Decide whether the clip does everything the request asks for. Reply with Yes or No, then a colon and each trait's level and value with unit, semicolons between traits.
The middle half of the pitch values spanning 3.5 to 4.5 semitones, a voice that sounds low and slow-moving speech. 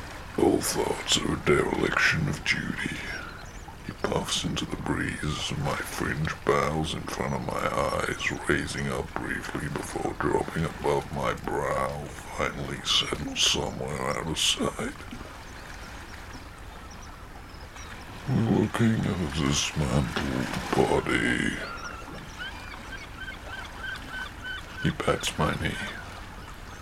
Yes: average, 4.2 semitones; very low, 85 Hz; slow, 100 wpm